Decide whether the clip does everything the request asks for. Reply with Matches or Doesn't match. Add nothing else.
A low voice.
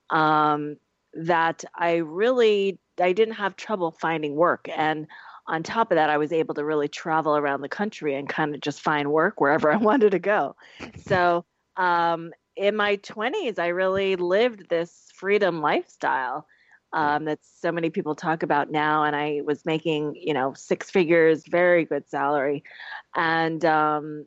Doesn't match